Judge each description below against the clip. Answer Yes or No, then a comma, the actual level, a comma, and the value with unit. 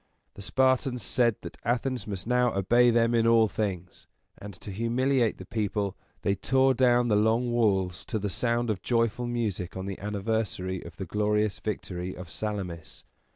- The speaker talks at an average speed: Yes, average, 170 wpm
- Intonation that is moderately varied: Yes, average, 3.5 semitones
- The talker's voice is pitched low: Yes, low, 110 Hz